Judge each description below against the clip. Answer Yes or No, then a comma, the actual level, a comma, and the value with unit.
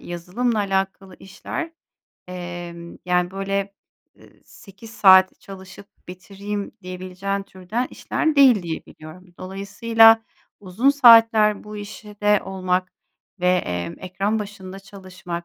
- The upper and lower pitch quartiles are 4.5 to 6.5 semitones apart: No, narrow, 2.4 semitones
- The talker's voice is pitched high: Yes, high, 195 Hz